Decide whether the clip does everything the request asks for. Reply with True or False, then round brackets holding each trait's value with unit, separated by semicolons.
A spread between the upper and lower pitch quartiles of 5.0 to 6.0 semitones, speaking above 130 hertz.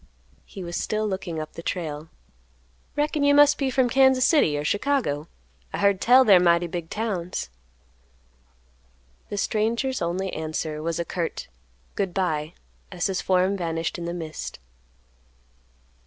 True (5.3 semitones; 185 Hz)